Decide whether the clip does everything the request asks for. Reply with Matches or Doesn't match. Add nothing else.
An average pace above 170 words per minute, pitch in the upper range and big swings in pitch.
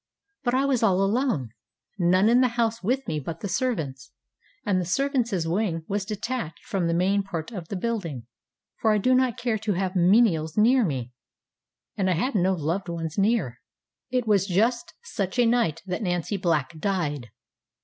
Matches